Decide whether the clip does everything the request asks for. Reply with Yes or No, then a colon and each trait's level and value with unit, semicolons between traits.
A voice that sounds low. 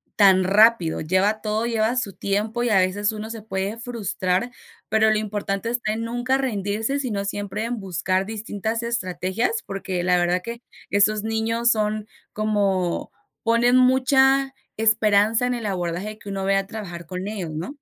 No: high, 215 Hz